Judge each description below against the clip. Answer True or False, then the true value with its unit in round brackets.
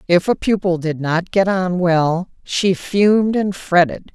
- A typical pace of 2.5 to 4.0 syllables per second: True (3.9 syllables/s)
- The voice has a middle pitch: True (180 Hz)